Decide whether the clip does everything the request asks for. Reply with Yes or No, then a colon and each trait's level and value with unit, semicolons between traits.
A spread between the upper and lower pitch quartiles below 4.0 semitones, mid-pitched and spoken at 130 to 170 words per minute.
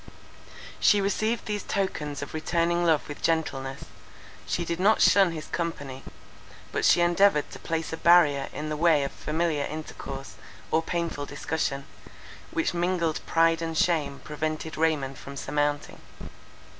Yes: average, 2.8 semitones; medium, 160 Hz; average, 145 wpm